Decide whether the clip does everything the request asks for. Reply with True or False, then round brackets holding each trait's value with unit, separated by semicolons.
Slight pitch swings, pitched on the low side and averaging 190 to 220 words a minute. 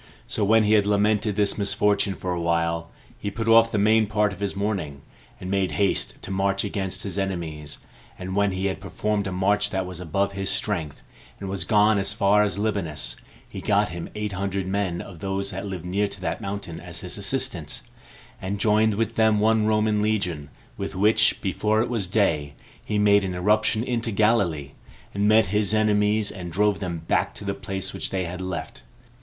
True (2.3 semitones; 100 Hz; 200 wpm)